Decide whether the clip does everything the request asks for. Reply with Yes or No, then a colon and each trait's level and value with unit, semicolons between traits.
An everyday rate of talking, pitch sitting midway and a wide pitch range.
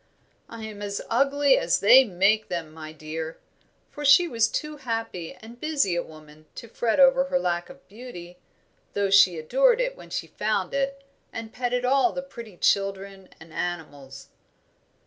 No: average, 165 wpm; high, 215 Hz; wide, 7.4 semitones